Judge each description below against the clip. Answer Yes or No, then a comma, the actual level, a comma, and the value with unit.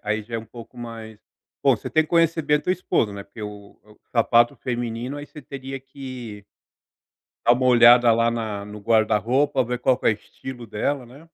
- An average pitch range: Yes, average, 3.3 semitones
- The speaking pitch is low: Yes, low, 120 Hz